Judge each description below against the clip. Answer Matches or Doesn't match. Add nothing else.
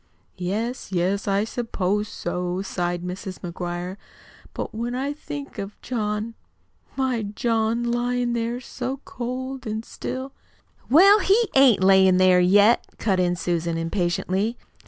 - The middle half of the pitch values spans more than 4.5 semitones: Matches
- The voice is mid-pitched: Doesn't match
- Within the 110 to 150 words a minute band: Matches